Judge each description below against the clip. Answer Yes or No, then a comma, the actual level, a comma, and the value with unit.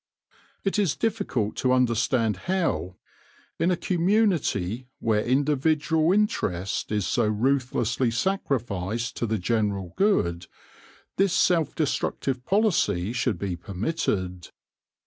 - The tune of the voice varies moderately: No, wide, 8.4 semitones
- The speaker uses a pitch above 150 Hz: No, low, 125 Hz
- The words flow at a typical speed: No, slow, 110 wpm